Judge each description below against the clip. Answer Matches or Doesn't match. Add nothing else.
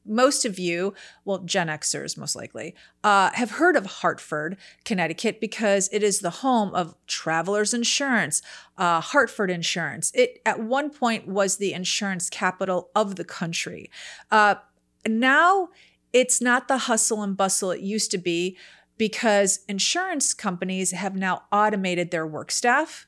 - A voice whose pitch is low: Doesn't match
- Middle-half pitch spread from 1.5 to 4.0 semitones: Doesn't match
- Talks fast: Doesn't match